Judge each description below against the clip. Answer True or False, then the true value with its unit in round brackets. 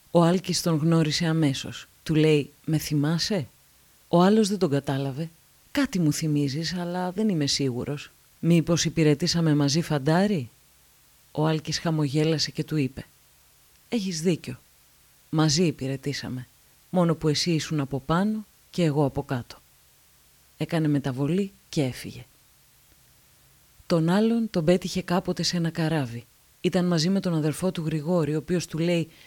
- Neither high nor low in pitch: True (160 Hz)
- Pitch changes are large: False (3.4 semitones)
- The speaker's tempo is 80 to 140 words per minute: True (135 wpm)